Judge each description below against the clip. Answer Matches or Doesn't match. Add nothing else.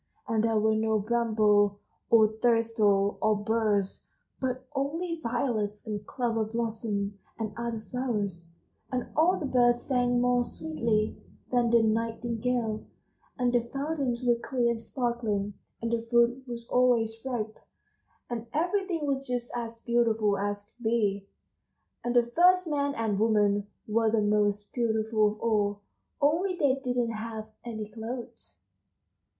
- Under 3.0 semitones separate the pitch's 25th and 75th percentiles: Matches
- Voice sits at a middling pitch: Doesn't match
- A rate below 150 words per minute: Matches